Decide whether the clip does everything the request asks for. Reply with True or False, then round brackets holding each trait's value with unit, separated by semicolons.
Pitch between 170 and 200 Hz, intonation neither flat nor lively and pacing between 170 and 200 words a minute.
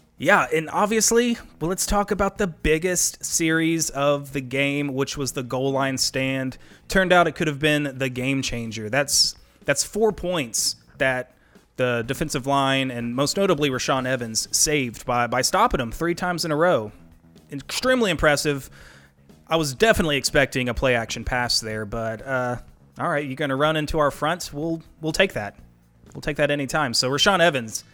False (140 Hz; 4.4 semitones; 175 wpm)